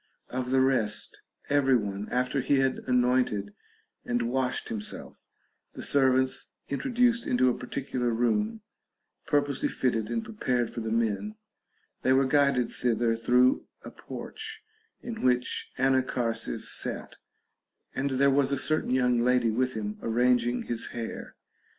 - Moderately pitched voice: No, low, 125 Hz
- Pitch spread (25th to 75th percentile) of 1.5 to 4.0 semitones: Yes, narrow, 2.4 semitones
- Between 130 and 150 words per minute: Yes, slow, 135 wpm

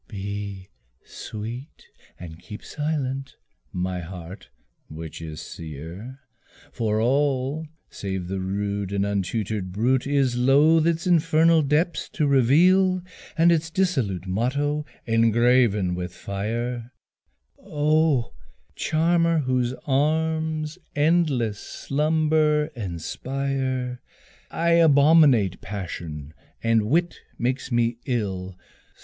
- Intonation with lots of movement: Yes, wide, 7.2 semitones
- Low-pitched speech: Yes, low, 125 Hz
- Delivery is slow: Yes, slow, 95 wpm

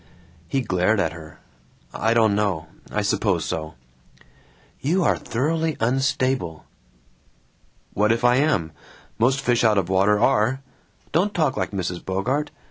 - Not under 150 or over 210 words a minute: No, slow, 135 wpm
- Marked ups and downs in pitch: Yes, wide, 5.9 semitones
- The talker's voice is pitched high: No, low, 115 Hz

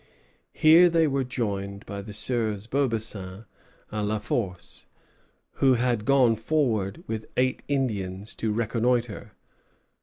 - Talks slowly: Yes, slow, 120 wpm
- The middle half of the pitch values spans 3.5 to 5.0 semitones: Yes, average, 4.0 semitones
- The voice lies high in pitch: No, low, 115 Hz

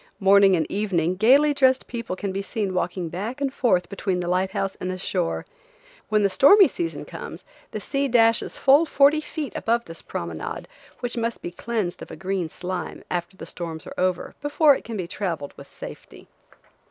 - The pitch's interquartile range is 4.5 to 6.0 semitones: Yes, wide, 5.5 semitones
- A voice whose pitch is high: Yes, high, 195 Hz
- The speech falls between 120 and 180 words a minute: No, average, 190 wpm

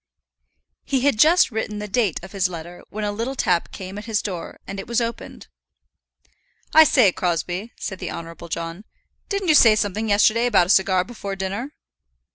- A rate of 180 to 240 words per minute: Yes, average, 185 wpm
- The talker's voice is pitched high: Yes, high, 205 Hz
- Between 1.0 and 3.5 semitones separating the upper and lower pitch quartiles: No, average, 4.2 semitones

